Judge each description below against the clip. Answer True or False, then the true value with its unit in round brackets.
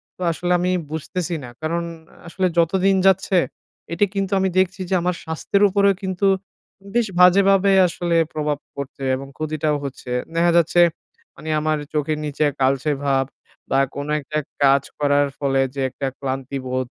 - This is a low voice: False (155 Hz)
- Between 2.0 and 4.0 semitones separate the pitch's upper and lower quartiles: False (4.6 semitones)